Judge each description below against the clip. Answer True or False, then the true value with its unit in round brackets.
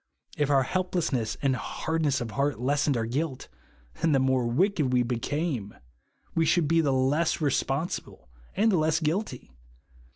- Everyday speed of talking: True (160 wpm)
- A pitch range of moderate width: True (4.0 semitones)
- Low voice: False (145 Hz)